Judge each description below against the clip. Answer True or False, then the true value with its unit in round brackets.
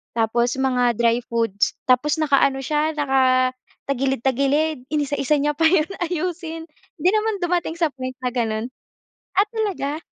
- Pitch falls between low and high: False (275 Hz)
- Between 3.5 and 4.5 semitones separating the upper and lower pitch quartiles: True (4.0 semitones)